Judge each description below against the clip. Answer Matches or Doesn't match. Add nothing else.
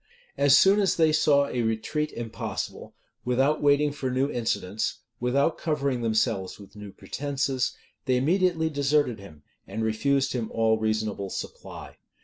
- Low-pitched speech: Matches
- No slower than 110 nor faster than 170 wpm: Matches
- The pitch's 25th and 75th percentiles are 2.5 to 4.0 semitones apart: Doesn't match